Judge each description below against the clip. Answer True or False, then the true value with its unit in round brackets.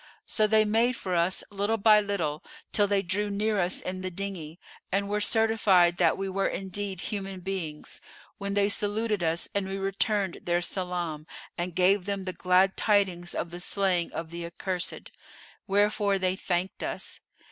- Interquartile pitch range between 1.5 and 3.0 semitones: True (2.4 semitones)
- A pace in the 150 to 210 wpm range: True (170 wpm)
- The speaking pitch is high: True (195 Hz)